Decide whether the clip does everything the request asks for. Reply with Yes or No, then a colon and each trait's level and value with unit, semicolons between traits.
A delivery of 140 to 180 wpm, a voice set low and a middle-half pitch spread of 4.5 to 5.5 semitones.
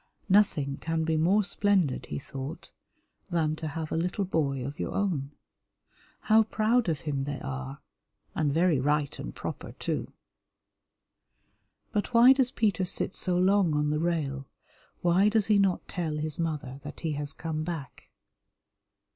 No: average, 155 wpm; medium, 160 Hz; average, 4.8 semitones